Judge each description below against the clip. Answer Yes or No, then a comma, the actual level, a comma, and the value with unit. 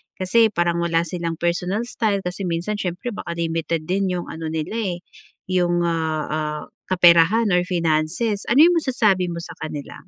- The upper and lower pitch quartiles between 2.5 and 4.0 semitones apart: Yes, average, 3.1 semitones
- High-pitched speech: No, medium, 175 Hz